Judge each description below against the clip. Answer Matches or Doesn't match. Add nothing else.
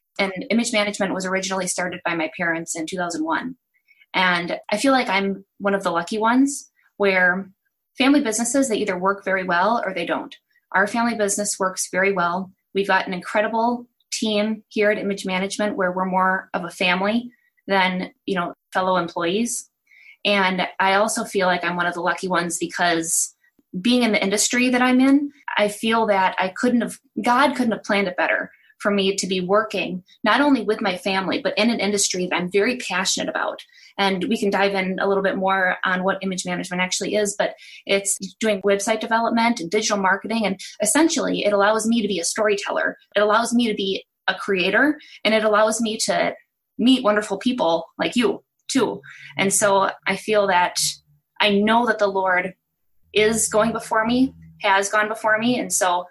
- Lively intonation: Doesn't match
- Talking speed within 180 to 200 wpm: Matches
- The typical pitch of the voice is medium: Doesn't match